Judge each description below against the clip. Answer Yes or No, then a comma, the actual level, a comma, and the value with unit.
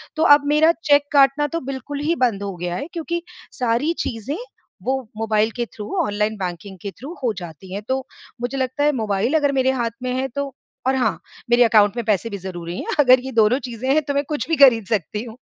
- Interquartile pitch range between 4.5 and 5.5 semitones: Yes, average, 5.0 semitones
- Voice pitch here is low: No, high, 245 Hz